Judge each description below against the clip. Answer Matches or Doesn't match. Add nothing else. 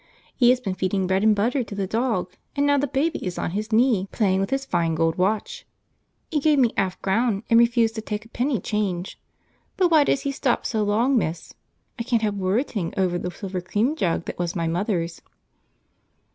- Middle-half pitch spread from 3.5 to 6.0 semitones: Matches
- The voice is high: Matches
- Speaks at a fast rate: Matches